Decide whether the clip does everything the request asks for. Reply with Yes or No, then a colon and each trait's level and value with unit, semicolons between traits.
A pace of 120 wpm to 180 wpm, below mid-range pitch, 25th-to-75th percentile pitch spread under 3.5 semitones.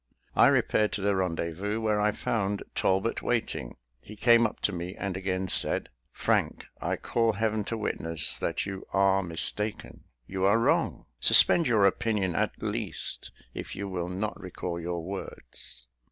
Yes: average, 160 wpm; low, 100 Hz; average, 2.7 semitones